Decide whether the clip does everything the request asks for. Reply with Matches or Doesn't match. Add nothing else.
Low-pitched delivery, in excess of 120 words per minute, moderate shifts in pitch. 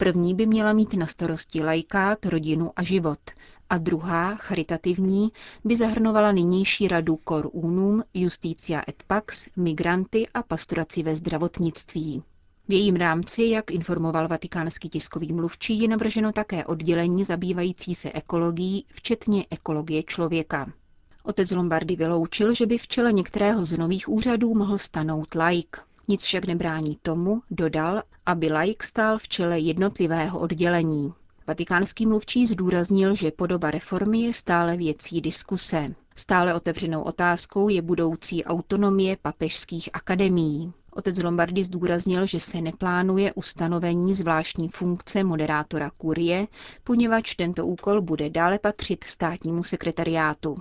Doesn't match